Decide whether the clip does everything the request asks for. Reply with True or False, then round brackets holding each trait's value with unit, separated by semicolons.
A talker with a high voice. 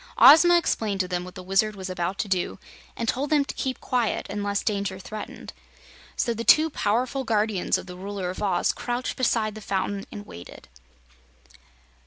True (210 Hz)